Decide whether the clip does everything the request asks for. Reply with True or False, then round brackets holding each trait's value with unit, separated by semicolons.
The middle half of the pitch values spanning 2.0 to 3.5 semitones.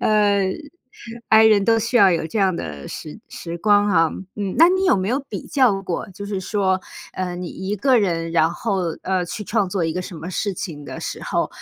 True (3.2 semitones)